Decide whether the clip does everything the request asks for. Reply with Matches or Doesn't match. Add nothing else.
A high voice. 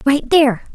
Matches